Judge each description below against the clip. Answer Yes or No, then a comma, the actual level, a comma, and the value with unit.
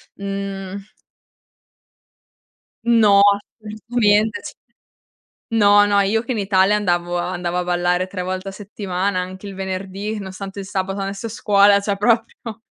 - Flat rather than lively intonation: Yes, narrow, 1.8 semitones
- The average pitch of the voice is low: No, high, 195 Hz